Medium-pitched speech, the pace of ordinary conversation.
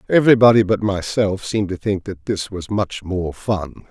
No: low, 100 Hz; average, 185 wpm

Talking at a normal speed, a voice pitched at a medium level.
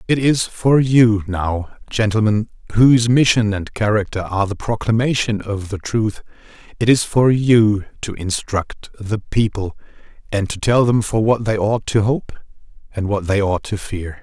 No: average, 170 wpm; low, 110 Hz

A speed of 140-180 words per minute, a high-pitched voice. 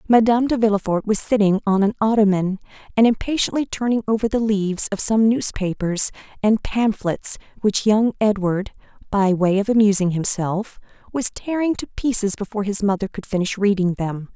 Yes: average, 160 wpm; high, 210 Hz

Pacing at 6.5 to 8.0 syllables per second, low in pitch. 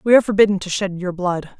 No: 6.7 syllables/s; high, 190 Hz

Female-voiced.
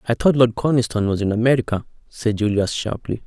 No: male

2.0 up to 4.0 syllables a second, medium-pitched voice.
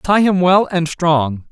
Yes: 3.4 syllables/s; medium, 170 Hz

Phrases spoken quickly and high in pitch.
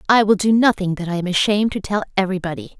Yes: fast, 235 wpm; high, 195 Hz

